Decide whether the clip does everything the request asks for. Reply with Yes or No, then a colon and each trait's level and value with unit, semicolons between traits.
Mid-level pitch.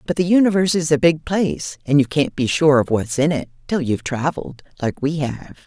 Yes: medium, 150 Hz